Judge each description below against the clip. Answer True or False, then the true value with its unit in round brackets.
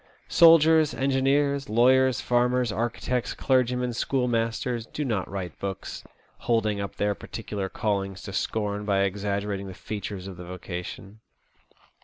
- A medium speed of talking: False (125 wpm)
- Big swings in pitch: False (4.2 semitones)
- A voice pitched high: False (110 Hz)